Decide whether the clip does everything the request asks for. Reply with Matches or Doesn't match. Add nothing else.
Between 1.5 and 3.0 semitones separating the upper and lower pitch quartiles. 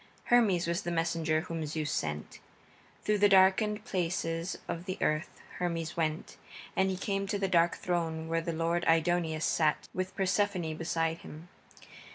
Matches